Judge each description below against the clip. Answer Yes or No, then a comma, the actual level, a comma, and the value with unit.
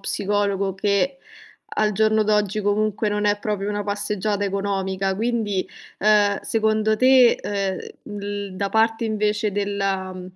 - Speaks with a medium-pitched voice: No, high, 205 Hz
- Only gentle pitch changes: Yes, narrow, 1.4 semitones